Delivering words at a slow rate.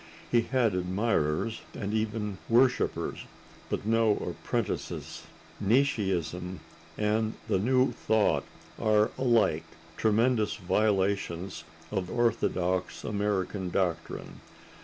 Yes: slow, 90 wpm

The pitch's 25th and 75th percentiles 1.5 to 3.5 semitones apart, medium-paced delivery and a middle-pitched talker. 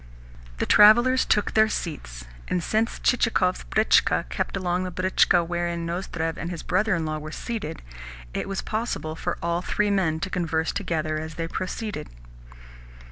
No: average, 4.2 semitones; average, 165 wpm; medium, 175 Hz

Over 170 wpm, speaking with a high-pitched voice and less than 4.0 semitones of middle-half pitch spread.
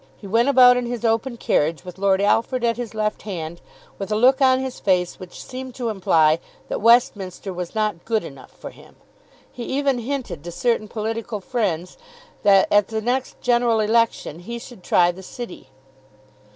No: average, 180 wpm; high, 220 Hz; average, 4.4 semitones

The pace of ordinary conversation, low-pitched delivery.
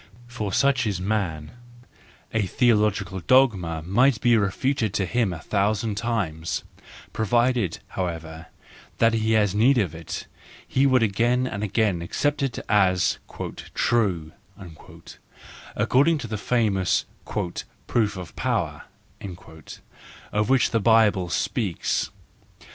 No: slow, 120 wpm; low, 105 Hz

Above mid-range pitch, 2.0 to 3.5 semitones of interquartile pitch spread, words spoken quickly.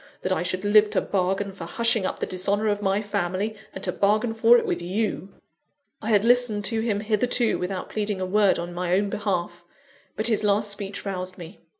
Yes: high, 205 Hz; narrow, 2.5 semitones; fast, 210 wpm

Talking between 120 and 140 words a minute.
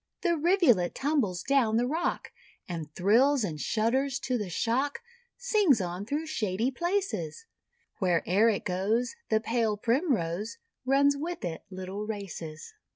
Yes: slow, 135 wpm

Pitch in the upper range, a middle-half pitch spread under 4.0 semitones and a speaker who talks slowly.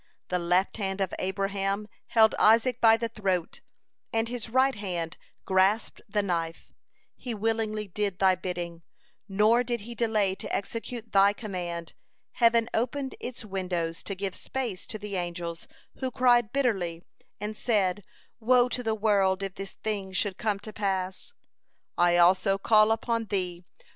No: high, 205 Hz; average, 3.4 semitones; average, 155 wpm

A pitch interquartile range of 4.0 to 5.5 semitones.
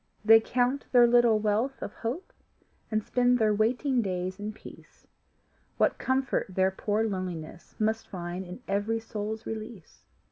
No: average, 3.6 semitones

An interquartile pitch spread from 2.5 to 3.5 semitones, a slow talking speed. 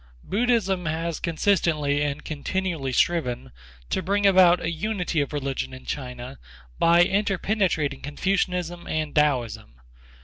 No: average, 4.7 semitones; slow, 115 wpm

